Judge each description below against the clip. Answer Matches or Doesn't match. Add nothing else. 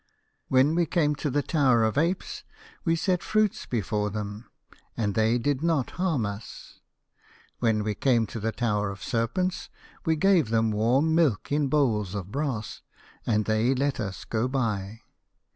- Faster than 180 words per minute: Doesn't match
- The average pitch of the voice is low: Matches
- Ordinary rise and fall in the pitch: Doesn't match